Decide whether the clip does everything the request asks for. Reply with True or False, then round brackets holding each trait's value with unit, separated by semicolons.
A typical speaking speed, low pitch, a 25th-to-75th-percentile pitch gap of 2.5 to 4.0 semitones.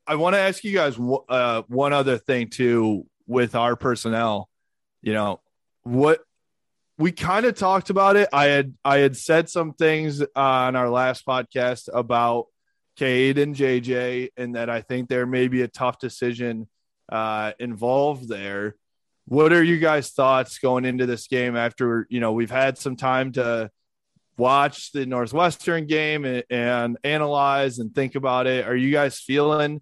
True (170 wpm; 130 Hz; 2.9 semitones)